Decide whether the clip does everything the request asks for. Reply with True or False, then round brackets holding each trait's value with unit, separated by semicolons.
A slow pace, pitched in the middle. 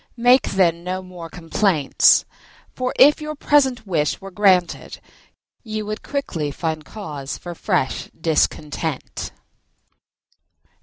True (110 wpm; 180 Hz)